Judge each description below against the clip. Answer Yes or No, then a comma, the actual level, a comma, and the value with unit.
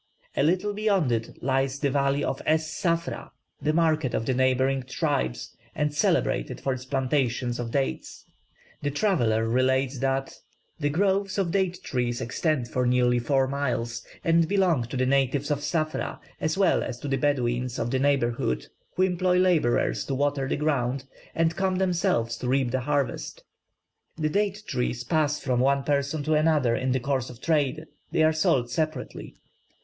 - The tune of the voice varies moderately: Yes, average, 3.9 semitones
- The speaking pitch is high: No, medium, 140 Hz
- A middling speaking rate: Yes, average, 170 wpm